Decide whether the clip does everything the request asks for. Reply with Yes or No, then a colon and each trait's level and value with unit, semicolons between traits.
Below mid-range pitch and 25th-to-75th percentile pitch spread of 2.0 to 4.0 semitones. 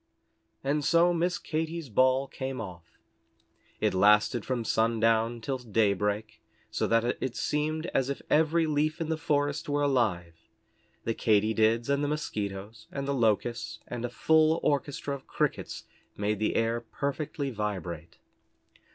No: low, 125 Hz; average, 5.1 semitones